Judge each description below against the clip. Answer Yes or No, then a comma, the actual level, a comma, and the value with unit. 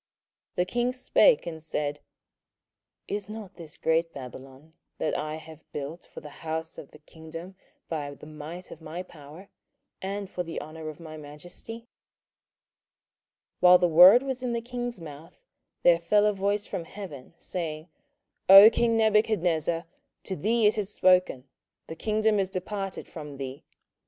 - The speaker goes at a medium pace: Yes, average, 160 wpm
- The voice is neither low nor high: Yes, medium, 175 Hz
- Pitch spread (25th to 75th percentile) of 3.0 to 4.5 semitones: No, average, 4.9 semitones